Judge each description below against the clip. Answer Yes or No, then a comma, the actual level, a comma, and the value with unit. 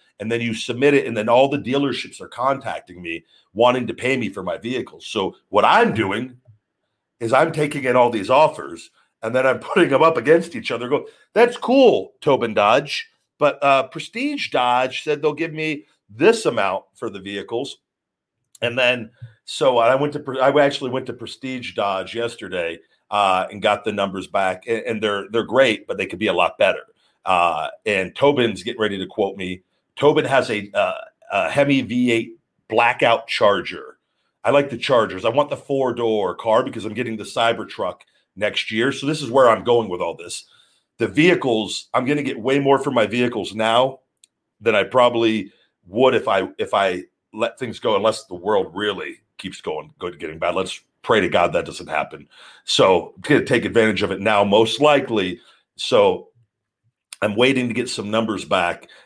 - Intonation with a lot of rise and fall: No, average, 4.4 semitones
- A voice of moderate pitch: No, low, 125 Hz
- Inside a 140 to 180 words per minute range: No, average, 190 wpm